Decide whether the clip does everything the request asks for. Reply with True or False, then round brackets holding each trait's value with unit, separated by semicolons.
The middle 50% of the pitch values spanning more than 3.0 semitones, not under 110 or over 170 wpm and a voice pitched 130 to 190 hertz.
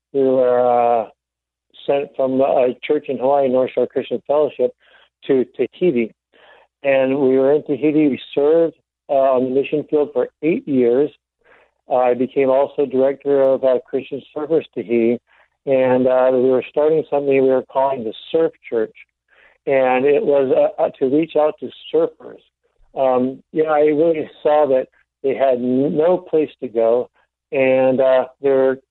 False (2.7 semitones; 165 wpm; 135 Hz)